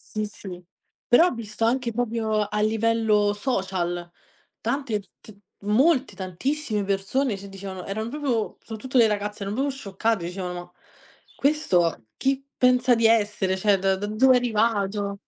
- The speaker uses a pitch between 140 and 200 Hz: No, high, 215 Hz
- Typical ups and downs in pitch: Yes, average, 3.8 semitones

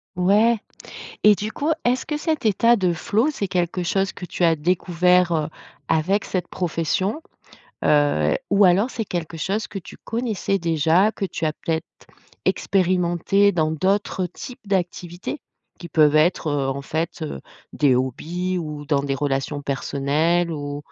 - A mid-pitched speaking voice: Yes, medium, 175 Hz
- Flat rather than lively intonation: No, average, 4.3 semitones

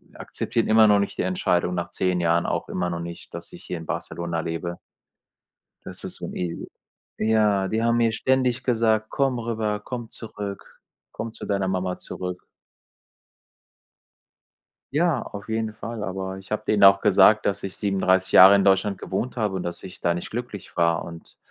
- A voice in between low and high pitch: No, low, 100 Hz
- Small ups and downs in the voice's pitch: No, average, 3.5 semitones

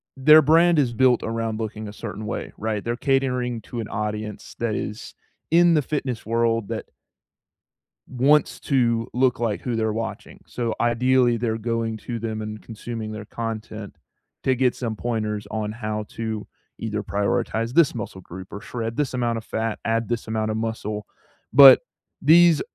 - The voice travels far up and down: No, narrow, 2.5 semitones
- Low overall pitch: Yes, low, 115 Hz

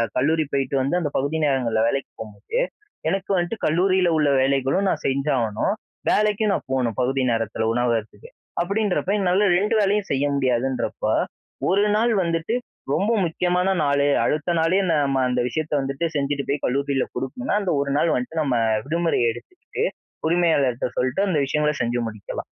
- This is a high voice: No, medium, 145 Hz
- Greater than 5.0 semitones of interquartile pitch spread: Yes, wide, 5.4 semitones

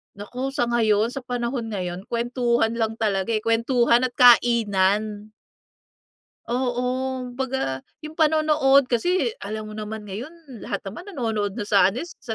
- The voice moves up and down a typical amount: Yes, average, 3.3 semitones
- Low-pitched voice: No, high, 235 Hz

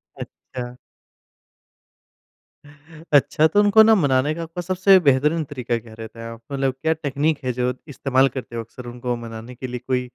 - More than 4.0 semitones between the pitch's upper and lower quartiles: Yes, average, 4.5 semitones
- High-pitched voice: No, low, 130 Hz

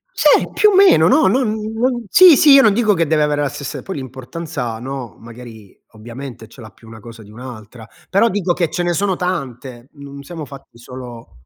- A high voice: No, medium, 140 Hz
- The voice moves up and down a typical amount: No, wide, 8.2 semitones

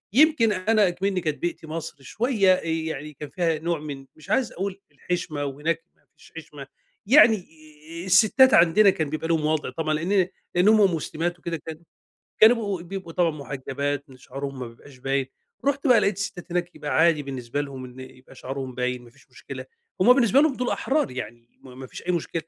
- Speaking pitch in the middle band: Yes, medium, 165 Hz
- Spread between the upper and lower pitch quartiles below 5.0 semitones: No, wide, 5.4 semitones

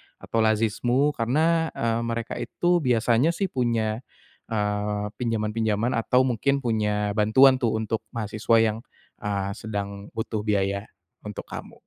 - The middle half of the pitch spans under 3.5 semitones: Yes, average, 2.8 semitones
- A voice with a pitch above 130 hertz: No, low, 115 Hz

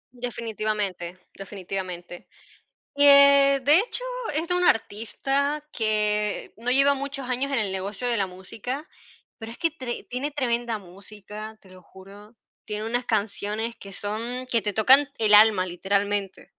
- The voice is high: Yes, high, 220 Hz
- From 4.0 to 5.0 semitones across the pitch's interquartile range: Yes, average, 4.6 semitones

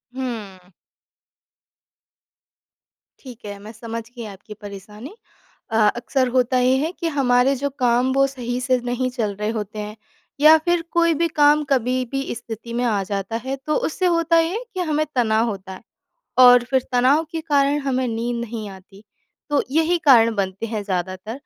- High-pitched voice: Yes, high, 245 Hz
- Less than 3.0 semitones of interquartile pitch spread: No, average, 4.3 semitones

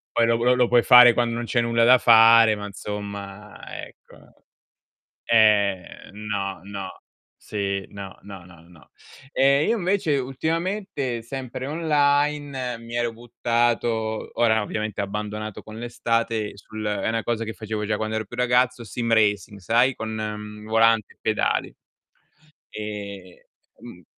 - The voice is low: Yes, low, 115 Hz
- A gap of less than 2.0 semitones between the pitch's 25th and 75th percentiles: No, average, 2.7 semitones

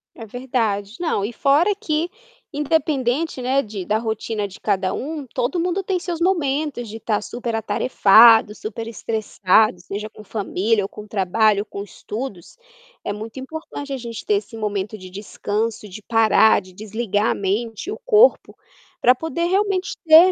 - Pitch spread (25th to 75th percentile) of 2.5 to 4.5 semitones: No, wide, 5.5 semitones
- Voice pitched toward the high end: Yes, high, 225 Hz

